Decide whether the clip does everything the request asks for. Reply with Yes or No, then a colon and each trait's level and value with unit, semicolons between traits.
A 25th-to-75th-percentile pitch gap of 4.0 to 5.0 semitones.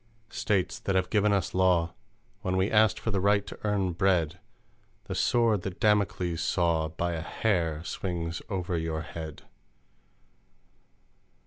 No: average, 3.3 semitones